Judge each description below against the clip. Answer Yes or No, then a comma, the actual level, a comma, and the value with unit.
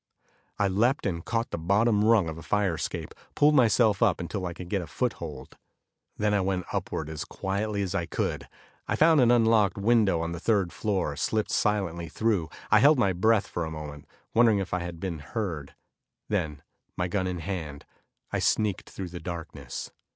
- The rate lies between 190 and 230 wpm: Yes, average, 195 wpm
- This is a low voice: Yes, very low, 95 Hz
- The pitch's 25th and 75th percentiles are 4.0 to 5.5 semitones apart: Yes, average, 4.3 semitones